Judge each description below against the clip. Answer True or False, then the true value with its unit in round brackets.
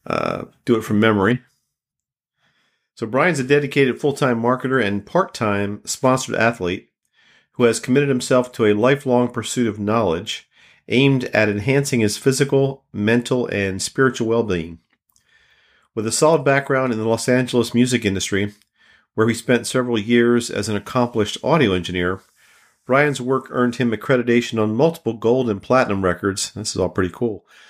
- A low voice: True (120 Hz)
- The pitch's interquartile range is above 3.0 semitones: True (3.7 semitones)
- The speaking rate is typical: True (150 wpm)